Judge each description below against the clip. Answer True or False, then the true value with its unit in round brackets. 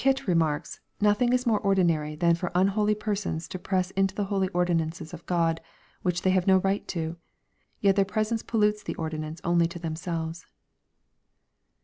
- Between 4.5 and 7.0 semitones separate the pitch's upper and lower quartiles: False (3.6 semitones)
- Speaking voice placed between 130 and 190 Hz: True (185 Hz)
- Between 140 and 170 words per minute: True (165 wpm)